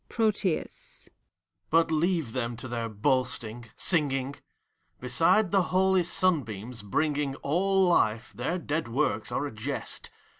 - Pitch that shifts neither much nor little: No, wide, 6.7 semitones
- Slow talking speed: Yes, slow, 120 wpm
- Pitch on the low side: No, medium, 145 Hz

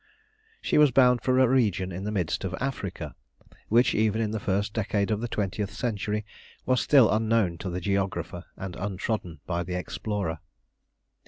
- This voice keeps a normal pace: Yes, average, 170 wpm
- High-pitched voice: No, low, 105 Hz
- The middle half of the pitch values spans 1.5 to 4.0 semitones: Yes, average, 3.6 semitones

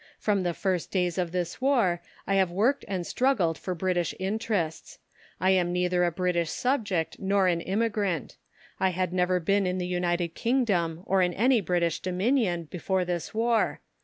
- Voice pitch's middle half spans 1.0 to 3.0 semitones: Yes, narrow, 2.5 semitones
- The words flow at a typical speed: Yes, average, 170 wpm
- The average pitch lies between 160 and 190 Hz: Yes, medium, 185 Hz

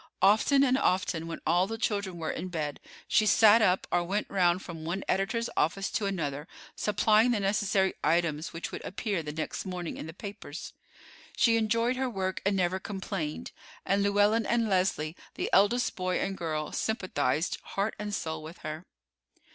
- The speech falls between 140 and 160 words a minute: No, average, 175 wpm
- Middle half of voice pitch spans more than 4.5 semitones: No, average, 3.9 semitones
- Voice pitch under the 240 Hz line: Yes, high, 190 Hz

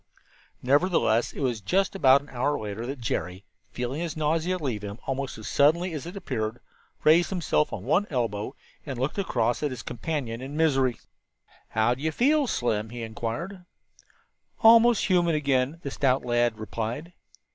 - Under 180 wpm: Yes, average, 170 wpm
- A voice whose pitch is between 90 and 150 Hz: Yes, low, 135 Hz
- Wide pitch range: Yes, wide, 5.8 semitones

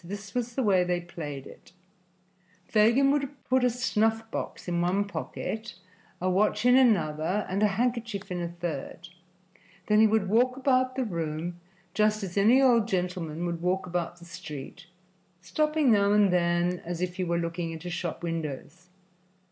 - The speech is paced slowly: No, average, 170 wpm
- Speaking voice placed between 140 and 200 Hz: Yes, medium, 185 Hz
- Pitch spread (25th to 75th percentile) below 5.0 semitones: Yes, average, 4.4 semitones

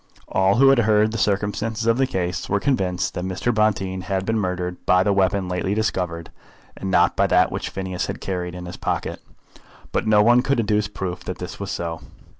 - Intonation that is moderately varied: Yes, average, 3.0 semitones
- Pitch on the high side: No, very low, 95 Hz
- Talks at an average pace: No, fast, 210 wpm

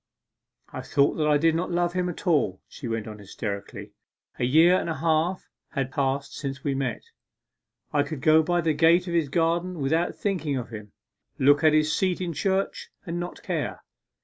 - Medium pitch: Yes, medium, 155 Hz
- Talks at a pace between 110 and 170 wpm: No, average, 195 wpm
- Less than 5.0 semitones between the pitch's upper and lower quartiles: Yes, average, 4.0 semitones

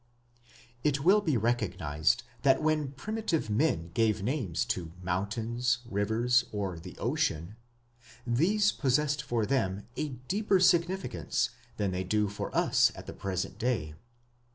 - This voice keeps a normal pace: No, slow, 130 wpm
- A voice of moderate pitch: No, low, 120 Hz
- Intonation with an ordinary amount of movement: No, wide, 7.3 semitones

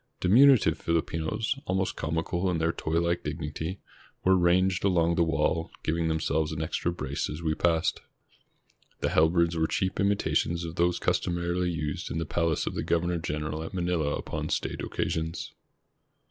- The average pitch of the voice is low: Yes, very low, 85 Hz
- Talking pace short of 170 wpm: Yes, average, 160 wpm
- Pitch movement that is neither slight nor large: No, narrow, 1.8 semitones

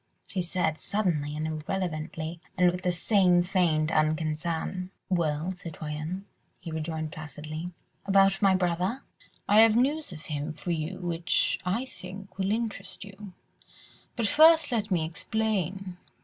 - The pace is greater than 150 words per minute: No, slow, 135 wpm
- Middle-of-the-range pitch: Yes, medium, 180 Hz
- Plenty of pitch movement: No, average, 3.7 semitones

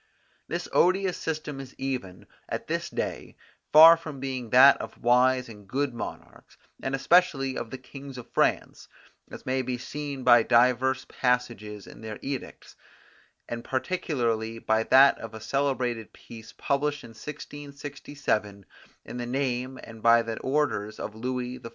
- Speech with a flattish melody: No, average, 3.2 semitones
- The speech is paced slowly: No, average, 150 wpm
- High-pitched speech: No, low, 130 Hz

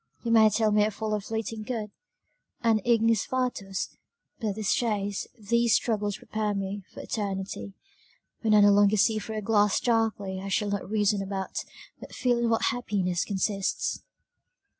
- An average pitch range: No, narrow, 2.1 semitones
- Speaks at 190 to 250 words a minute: No, average, 165 wpm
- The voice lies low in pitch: No, high, 210 Hz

